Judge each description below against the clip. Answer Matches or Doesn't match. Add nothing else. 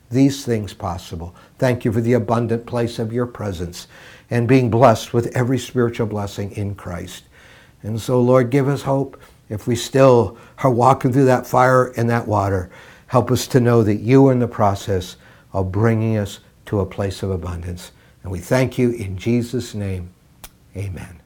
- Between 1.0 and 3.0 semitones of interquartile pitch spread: Doesn't match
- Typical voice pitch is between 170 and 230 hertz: Doesn't match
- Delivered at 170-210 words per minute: Matches